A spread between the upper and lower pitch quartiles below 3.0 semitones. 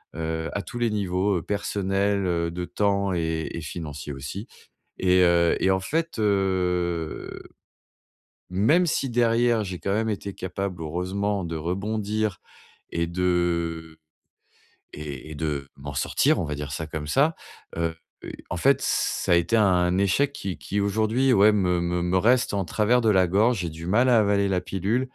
No: average, 3.7 semitones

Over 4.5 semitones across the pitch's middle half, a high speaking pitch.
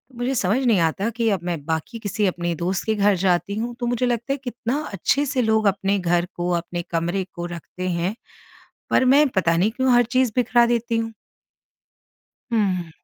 Yes: wide, 5.4 semitones; high, 205 Hz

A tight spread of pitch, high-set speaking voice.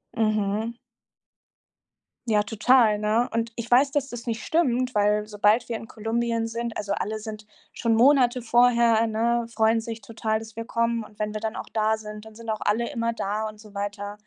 Yes: narrow, 1.8 semitones; high, 225 Hz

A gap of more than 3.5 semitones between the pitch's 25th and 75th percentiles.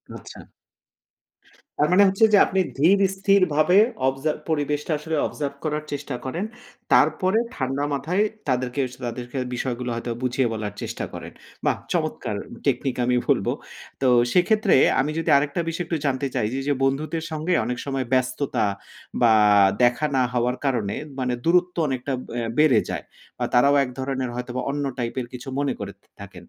Yes: average, 3.9 semitones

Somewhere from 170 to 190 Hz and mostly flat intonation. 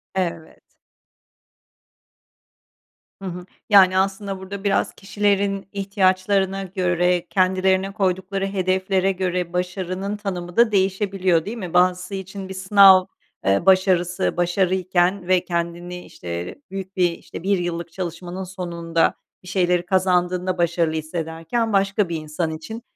Yes: medium, 185 Hz; narrow, 1.7 semitones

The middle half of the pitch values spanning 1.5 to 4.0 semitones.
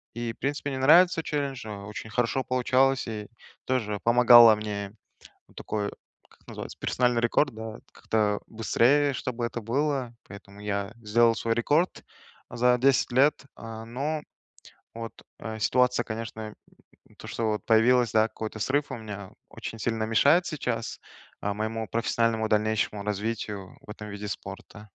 Yes: average, 2.8 semitones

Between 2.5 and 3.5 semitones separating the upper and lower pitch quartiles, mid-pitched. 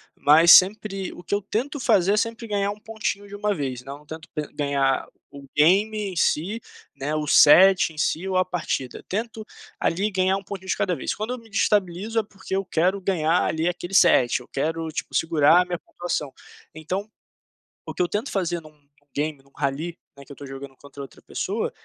No: average, 5.0 semitones; medium, 175 Hz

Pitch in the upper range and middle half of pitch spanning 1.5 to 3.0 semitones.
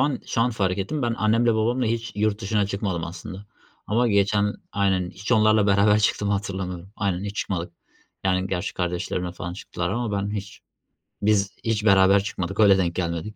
No: low, 100 Hz; narrow, 2.5 semitones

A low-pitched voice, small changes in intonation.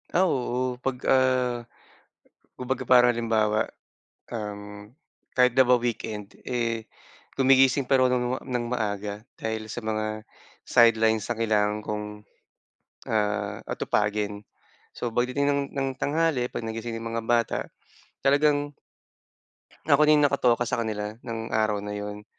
No: low, 115 Hz; average, 3.1 semitones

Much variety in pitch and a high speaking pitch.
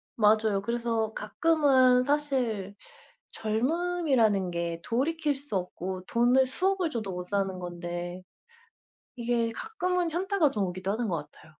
Yes: wide, 7.0 semitones; high, 230 Hz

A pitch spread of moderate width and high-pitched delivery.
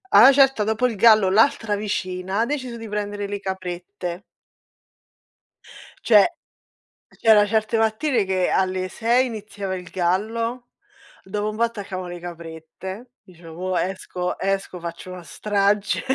Yes: average, 3.2 semitones; high, 205 Hz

